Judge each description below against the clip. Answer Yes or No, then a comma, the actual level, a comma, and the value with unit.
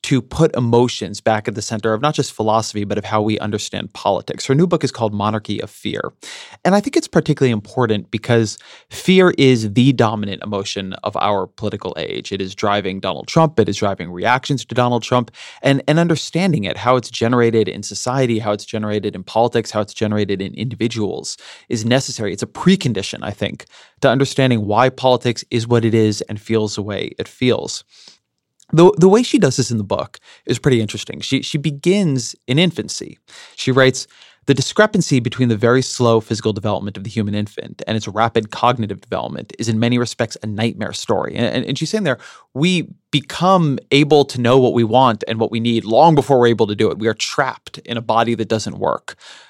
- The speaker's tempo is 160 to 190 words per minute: No, fast, 205 wpm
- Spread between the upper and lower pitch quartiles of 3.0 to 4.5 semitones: Yes, average, 3.9 semitones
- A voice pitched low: Yes, low, 120 Hz